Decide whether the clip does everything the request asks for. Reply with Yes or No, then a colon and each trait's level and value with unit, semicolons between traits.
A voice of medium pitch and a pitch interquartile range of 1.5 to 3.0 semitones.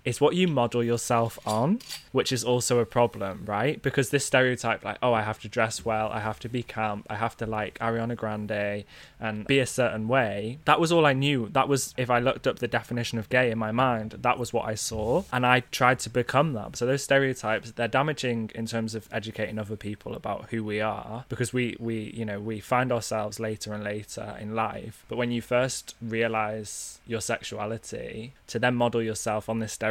No: low, 115 Hz; narrow, 2.4 semitones